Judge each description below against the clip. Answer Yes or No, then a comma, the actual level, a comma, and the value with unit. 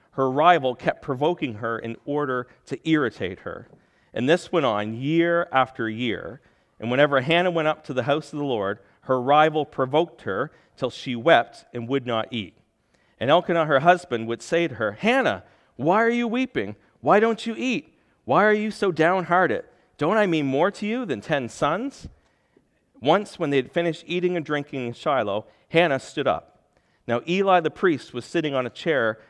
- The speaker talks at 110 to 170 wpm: No, average, 190 wpm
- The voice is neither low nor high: Yes, medium, 150 Hz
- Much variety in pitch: Yes, wide, 5.9 semitones